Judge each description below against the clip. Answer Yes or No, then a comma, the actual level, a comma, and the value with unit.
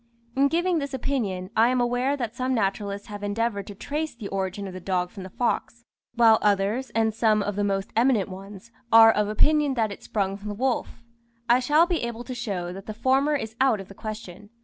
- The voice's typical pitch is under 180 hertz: No, high, 220 Hz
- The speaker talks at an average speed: No, fast, 220 wpm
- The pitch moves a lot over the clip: No, average, 4.1 semitones